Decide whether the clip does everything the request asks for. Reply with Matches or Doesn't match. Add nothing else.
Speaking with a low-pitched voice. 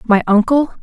Doesn't match